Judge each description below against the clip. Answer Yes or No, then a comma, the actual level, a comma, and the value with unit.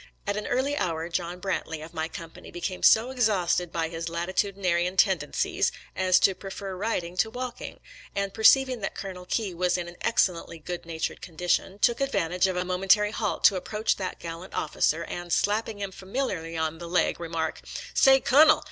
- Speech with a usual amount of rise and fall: Yes, average, 3.6 semitones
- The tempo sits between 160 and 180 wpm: No, average, 190 wpm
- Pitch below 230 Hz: Yes, medium, 185 Hz